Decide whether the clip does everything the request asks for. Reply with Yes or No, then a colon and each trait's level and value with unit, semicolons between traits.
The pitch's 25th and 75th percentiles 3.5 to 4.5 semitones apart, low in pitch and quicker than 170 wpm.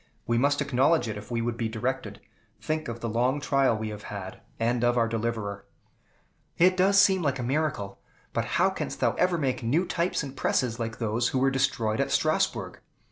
Yes: average, 3.9 semitones; low, 120 Hz; average, 200 wpm